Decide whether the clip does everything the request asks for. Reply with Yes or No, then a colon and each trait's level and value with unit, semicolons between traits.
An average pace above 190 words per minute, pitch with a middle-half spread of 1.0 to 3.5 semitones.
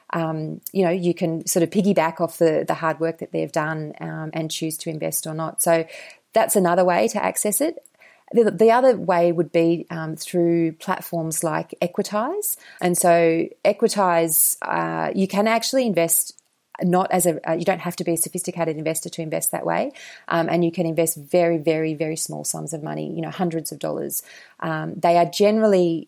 Yes: average, 200 wpm; narrow, 2.6 semitones